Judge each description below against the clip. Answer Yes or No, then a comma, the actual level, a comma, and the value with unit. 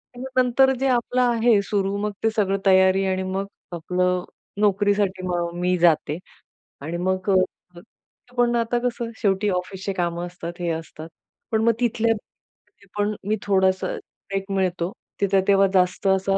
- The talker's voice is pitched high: Yes, high, 195 Hz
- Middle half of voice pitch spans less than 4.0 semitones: Yes, average, 2.8 semitones